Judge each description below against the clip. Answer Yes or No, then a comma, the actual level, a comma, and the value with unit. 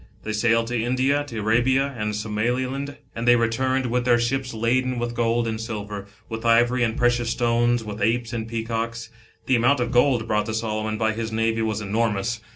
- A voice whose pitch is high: No, low, 115 Hz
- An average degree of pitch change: No, narrow, 1.6 semitones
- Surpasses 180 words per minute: Yes, average, 190 wpm